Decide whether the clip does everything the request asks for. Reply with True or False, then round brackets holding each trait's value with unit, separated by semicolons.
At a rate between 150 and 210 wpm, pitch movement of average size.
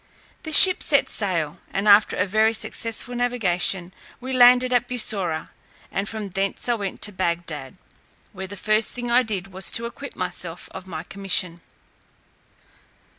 True (155 wpm; 4.6 semitones)